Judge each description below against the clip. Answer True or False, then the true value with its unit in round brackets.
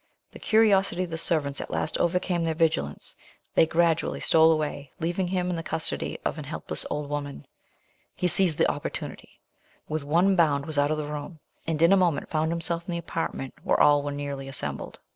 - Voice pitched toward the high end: False (160 Hz)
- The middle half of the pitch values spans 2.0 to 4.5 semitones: True (2.9 semitones)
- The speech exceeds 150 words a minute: True (200 wpm)